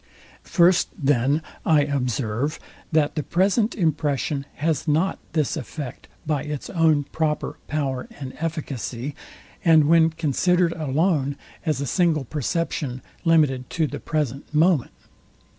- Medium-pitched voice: Yes, medium, 150 Hz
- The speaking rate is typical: No, slow, 125 wpm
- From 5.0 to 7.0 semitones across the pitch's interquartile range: No, average, 3.0 semitones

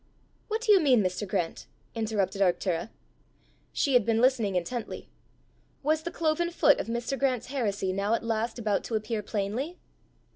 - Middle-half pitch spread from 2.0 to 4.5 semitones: No, average, 5.2 semitones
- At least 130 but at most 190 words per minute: Yes, average, 160 wpm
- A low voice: No, high, 230 Hz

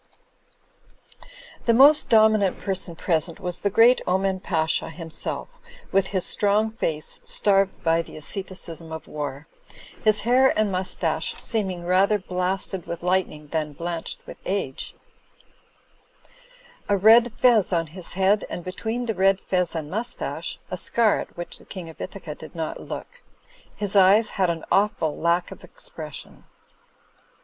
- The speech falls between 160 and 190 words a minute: No, average, 145 wpm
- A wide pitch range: No, average, 3.9 semitones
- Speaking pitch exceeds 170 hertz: Yes, medium, 185 Hz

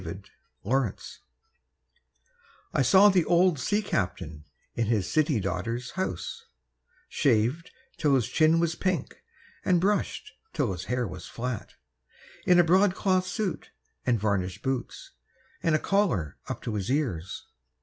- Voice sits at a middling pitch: No, low, 130 Hz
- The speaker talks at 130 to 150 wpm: Yes, slow, 135 wpm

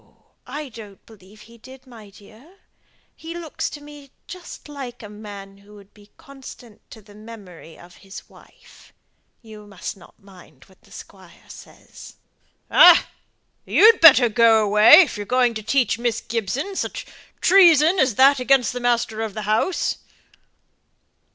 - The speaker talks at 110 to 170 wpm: Yes, average, 155 wpm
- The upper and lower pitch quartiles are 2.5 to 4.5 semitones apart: No, average, 4.9 semitones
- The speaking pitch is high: Yes, high, 230 Hz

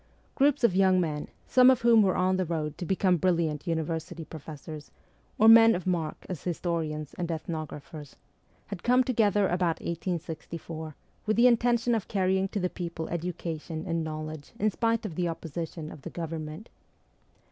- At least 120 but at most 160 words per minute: No, average, 170 wpm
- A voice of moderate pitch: Yes, medium, 175 Hz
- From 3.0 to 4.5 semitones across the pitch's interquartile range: Yes, average, 3.8 semitones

